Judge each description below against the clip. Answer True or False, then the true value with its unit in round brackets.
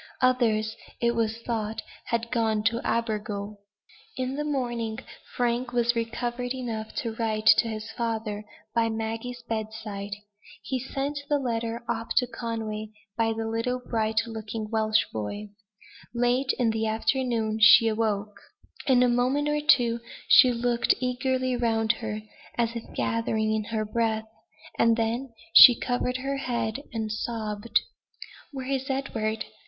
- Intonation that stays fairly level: True (2.1 semitones)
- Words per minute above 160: False (140 wpm)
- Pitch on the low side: False (230 Hz)